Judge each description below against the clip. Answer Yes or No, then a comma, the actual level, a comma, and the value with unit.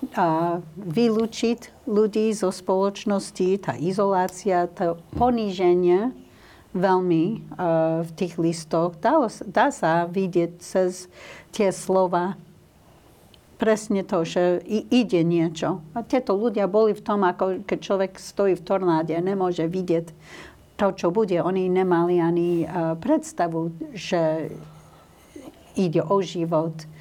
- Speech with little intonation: No, average, 3.0 semitones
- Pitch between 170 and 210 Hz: Yes, medium, 185 Hz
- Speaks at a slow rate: No, average, 120 wpm